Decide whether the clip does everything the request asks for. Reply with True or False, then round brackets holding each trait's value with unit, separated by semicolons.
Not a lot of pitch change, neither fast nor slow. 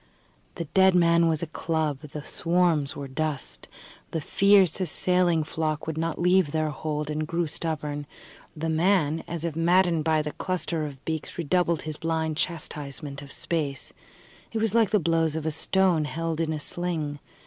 True (2.3 semitones; 170 wpm)